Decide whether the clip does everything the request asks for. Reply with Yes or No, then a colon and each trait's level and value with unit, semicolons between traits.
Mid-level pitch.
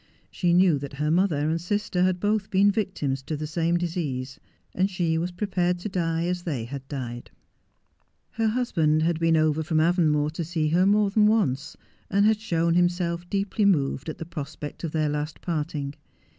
Yes: medium, 170 Hz